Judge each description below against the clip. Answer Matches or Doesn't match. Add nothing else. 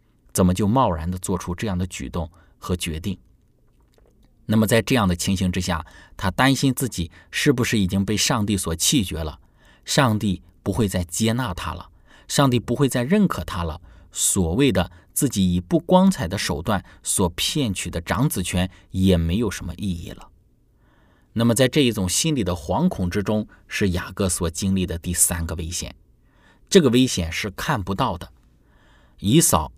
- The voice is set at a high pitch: Doesn't match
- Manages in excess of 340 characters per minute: Doesn't match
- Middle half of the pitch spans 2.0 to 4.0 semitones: Doesn't match